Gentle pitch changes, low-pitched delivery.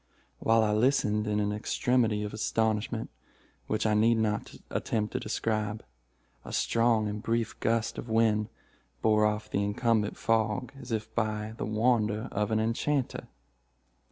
Yes: narrow, 1.4 semitones; low, 110 Hz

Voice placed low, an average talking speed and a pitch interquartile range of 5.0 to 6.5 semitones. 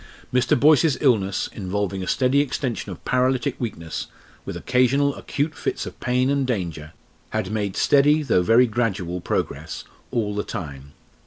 Yes: low, 120 Hz; average, 150 wpm; wide, 5.6 semitones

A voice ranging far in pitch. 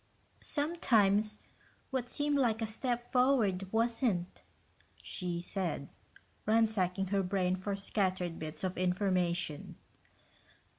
No: average, 4.0 semitones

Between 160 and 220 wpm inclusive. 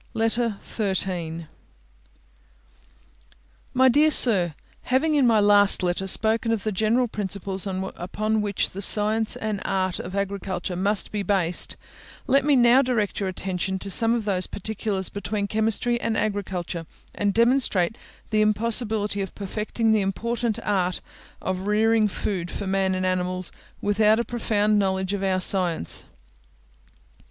No: average, 140 wpm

